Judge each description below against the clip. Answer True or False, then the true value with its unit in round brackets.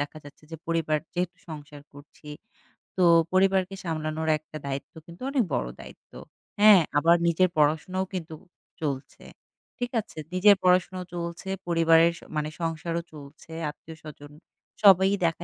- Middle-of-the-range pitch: True (165 Hz)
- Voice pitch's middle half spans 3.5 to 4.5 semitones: False (3.1 semitones)